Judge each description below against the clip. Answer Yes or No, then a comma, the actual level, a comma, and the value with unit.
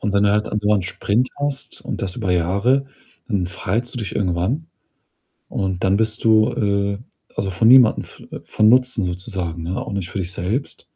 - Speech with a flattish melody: No, average, 3.3 semitones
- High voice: No, low, 100 Hz